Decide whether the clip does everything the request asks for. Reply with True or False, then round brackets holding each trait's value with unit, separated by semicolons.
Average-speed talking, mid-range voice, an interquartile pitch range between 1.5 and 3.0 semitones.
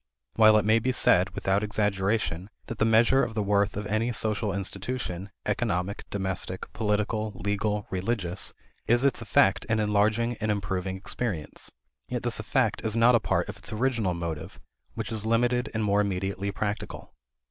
False (165 wpm; 105 Hz; 2.6 semitones)